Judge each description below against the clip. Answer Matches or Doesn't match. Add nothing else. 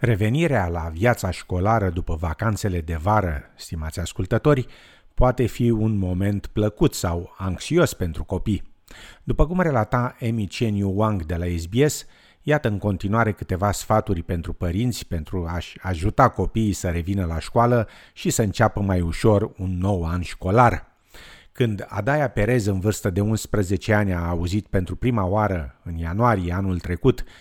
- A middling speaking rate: Matches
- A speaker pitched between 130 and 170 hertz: Doesn't match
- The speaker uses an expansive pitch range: Doesn't match